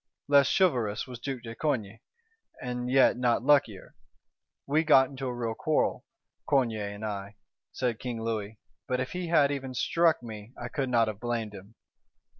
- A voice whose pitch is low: Yes, low, 125 Hz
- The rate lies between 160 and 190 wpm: Yes, average, 170 wpm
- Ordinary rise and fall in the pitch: Yes, average, 3.6 semitones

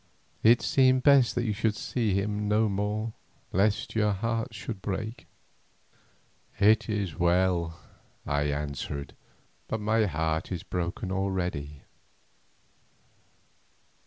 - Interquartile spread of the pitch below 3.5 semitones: No, average, 4.1 semitones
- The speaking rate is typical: No, slow, 110 wpm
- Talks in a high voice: No, low, 100 Hz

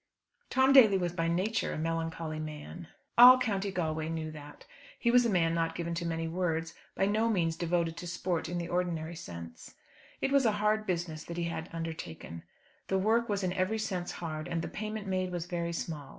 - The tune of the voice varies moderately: Yes, average, 3.3 semitones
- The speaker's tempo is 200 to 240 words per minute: Yes, fast, 205 wpm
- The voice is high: No, medium, 170 Hz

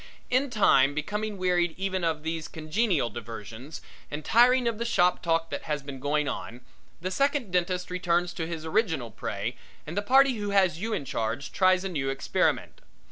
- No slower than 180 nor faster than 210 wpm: Yes, average, 185 wpm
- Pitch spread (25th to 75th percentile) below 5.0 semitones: No, wide, 5.5 semitones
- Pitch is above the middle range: No, medium, 175 Hz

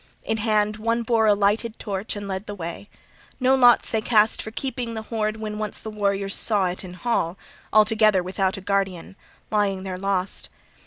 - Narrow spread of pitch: Yes, narrow, 2.3 semitones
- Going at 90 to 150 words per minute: No, average, 190 wpm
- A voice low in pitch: No, high, 210 Hz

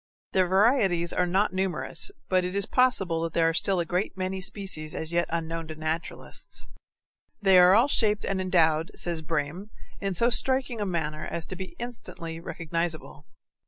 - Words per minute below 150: No, average, 175 wpm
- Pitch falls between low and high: Yes, medium, 180 Hz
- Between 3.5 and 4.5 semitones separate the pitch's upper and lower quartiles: No, average, 3.0 semitones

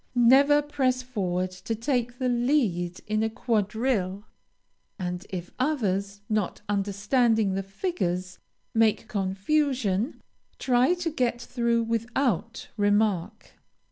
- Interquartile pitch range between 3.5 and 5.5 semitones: Yes, average, 4.5 semitones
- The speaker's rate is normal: No, slow, 110 wpm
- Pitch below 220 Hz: No, high, 225 Hz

